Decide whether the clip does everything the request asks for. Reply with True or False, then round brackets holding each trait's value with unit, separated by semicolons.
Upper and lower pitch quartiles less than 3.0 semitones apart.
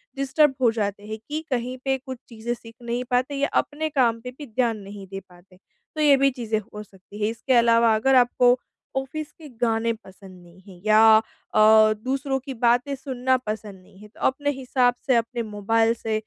False (3.6 semitones)